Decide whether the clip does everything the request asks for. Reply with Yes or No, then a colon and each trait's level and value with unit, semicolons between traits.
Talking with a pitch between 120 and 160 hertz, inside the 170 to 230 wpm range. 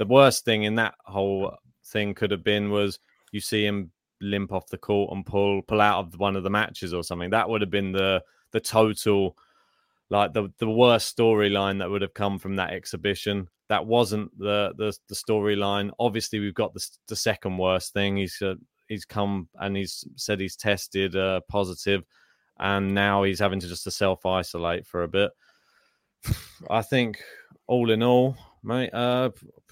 No: low, 100 Hz; average, 185 wpm